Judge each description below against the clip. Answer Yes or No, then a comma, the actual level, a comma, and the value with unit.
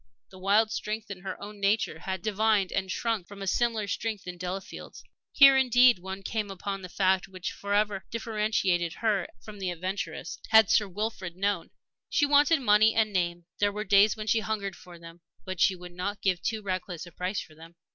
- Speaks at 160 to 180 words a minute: No, average, 195 wpm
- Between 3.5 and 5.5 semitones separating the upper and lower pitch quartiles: No, average, 2.7 semitones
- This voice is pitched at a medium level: No, high, 200 Hz